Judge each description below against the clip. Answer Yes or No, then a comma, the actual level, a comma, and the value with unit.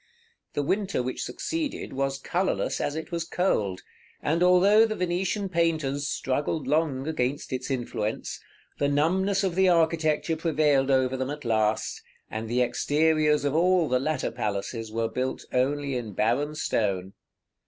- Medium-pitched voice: Yes, medium, 145 Hz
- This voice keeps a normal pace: Yes, average, 150 wpm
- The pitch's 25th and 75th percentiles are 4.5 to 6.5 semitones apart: Yes, average, 4.8 semitones